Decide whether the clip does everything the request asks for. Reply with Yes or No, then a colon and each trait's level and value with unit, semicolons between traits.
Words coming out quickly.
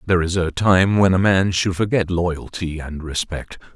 No: average, 190 wpm